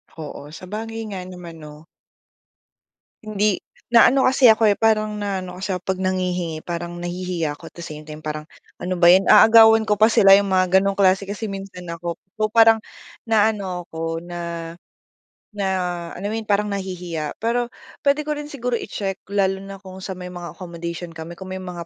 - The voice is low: No, high, 190 Hz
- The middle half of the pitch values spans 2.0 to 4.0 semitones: Yes, average, 3.6 semitones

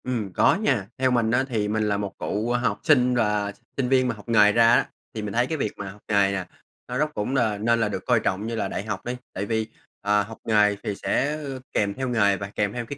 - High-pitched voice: No, low, 110 Hz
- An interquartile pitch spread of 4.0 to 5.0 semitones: No, average, 3.2 semitones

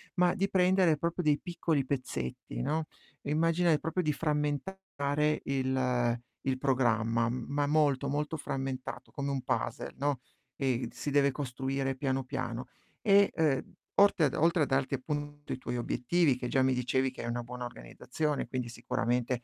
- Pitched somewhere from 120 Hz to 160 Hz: Yes, medium, 140 Hz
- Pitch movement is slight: No, average, 3.3 semitones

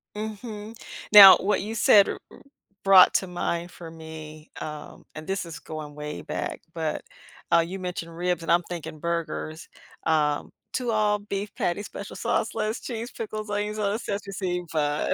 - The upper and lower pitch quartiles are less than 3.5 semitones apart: No, average, 4.4 semitones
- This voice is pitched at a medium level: Yes, medium, 180 Hz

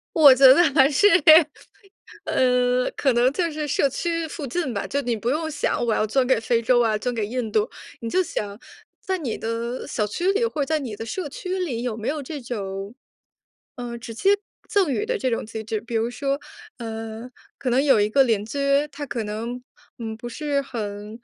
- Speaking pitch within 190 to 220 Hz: No, high, 245 Hz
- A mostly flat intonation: No, average, 4.4 semitones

